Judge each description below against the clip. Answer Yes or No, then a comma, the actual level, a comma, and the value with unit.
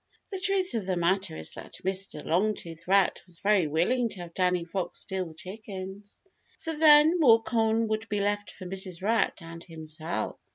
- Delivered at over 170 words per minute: Yes, average, 180 wpm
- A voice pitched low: No, high, 190 Hz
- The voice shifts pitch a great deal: No, average, 4.3 semitones